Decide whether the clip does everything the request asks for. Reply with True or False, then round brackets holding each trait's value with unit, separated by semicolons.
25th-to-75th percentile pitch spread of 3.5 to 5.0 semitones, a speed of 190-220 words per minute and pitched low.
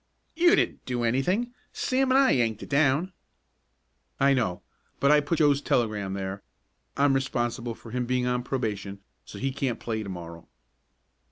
False (4.5 semitones; 165 wpm; 125 Hz)